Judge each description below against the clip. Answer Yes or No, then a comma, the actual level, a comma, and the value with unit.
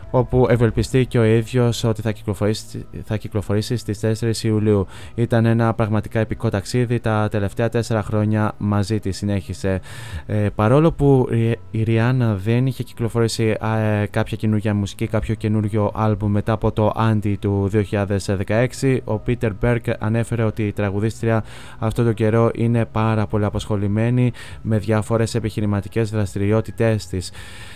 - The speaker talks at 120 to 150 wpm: Yes, average, 140 wpm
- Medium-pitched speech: No, low, 110 Hz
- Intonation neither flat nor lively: No, narrow, 1.6 semitones